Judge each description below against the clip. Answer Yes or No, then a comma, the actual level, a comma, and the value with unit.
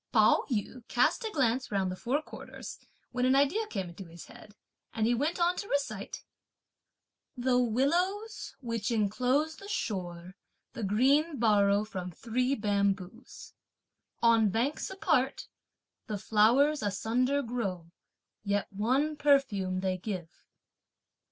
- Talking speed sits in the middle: No, slow, 130 wpm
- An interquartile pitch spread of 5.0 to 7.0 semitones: Yes, wide, 5.6 semitones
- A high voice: Yes, high, 235 Hz